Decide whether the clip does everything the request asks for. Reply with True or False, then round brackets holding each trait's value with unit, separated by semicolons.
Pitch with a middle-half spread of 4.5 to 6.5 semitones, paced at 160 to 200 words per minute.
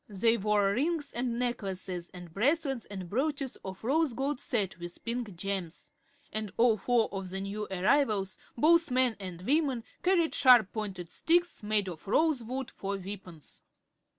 False (5.4 semitones; 150 wpm)